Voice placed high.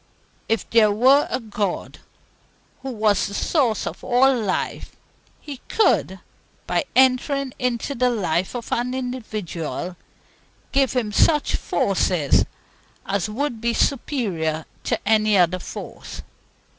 Yes: high, 230 Hz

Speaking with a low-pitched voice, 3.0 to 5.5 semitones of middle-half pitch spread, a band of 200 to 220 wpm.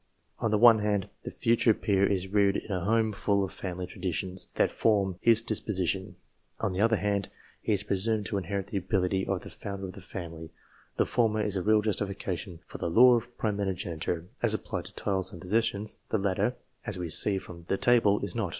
No: low, 100 Hz; narrow, 2.5 semitones; fast, 205 wpm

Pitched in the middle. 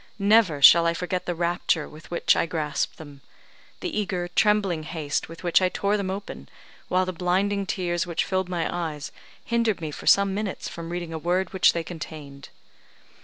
Yes: medium, 175 Hz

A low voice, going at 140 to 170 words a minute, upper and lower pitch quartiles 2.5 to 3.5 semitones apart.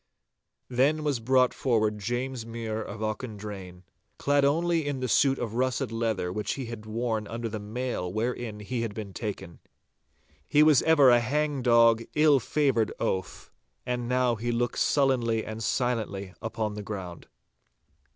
Yes: low, 115 Hz; average, 150 wpm; average, 3.2 semitones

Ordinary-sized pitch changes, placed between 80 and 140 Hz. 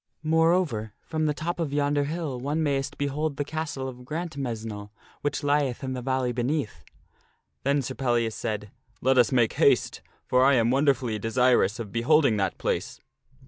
Yes: average, 3.8 semitones; low, 135 Hz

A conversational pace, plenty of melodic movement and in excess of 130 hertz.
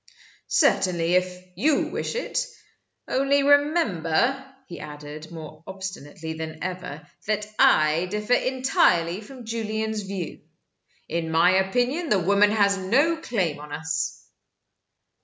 No: slow, 120 wpm; wide, 7.0 semitones; high, 190 Hz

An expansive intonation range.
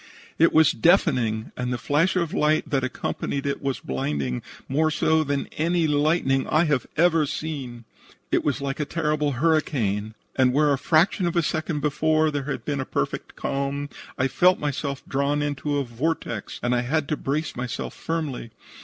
No: average, 3.1 semitones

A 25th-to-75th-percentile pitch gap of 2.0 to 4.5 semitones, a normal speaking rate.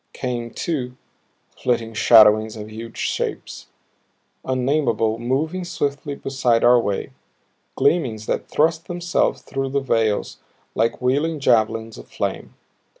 No: average, 3.9 semitones; slow, 115 wpm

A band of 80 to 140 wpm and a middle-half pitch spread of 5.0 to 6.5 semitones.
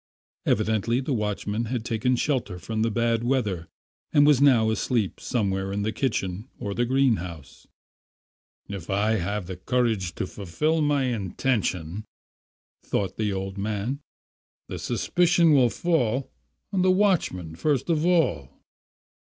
Yes: slow, 135 wpm; average, 5.3 semitones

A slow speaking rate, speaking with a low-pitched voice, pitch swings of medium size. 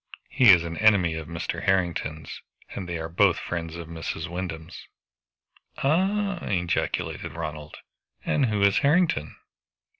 Yes: slow, 130 wpm; very low, 85 Hz; average, 4.2 semitones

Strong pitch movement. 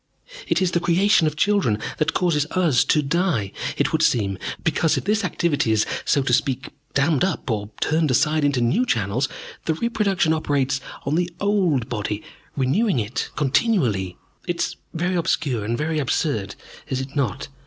Yes: wide, 5.9 semitones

